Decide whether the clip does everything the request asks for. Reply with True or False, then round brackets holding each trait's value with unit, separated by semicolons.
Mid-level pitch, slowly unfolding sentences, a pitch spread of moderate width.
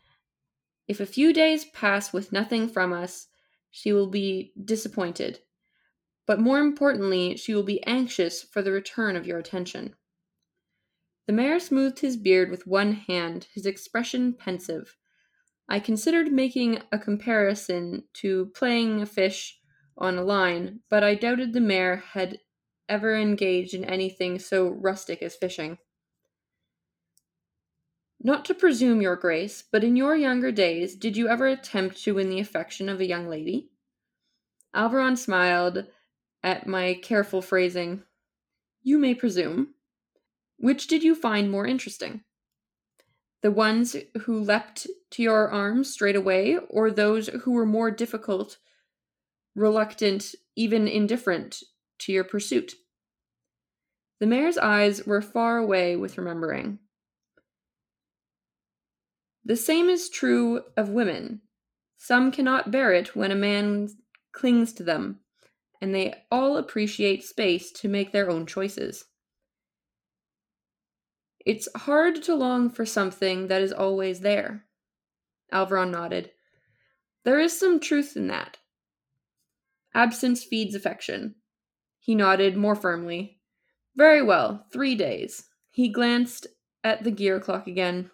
False (210 Hz; 130 wpm; 4.3 semitones)